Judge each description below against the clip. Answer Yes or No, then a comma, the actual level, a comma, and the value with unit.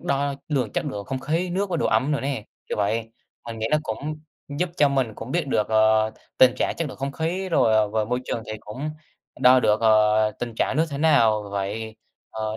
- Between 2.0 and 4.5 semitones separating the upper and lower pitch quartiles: No, average, 5.0 semitones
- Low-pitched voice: Yes, low, 125 Hz